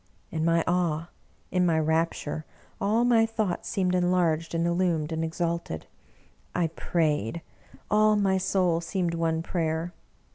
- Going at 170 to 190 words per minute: No, average, 140 wpm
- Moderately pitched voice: Yes, medium, 170 Hz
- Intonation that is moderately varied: No, narrow, 2.1 semitones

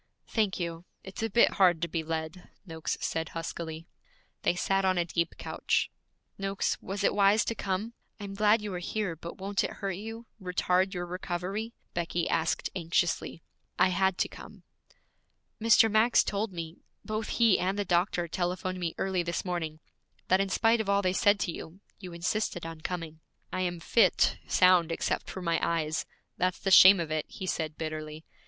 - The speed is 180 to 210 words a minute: Yes, average, 185 wpm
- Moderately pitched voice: Yes, medium, 180 Hz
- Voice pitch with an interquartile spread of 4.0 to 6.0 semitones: No, average, 2.9 semitones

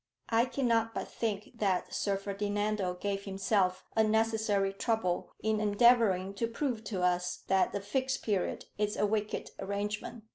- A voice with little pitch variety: Yes, narrow, 2.3 semitones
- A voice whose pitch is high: Yes, high, 210 Hz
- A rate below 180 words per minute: Yes, average, 145 wpm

